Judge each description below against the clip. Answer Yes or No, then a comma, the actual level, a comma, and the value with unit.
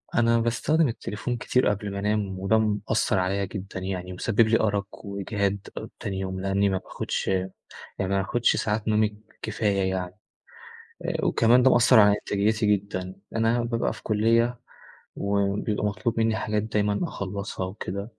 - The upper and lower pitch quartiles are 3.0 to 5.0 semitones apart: No, narrow, 2.4 semitones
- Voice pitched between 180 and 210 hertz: No, low, 105 Hz